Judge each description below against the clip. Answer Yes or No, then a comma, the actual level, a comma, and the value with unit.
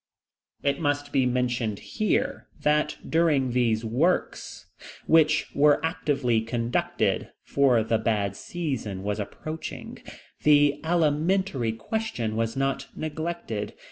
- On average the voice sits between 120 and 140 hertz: Yes, low, 135 Hz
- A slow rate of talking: Yes, slow, 110 wpm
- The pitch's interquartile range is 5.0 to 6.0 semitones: Yes, wide, 5.4 semitones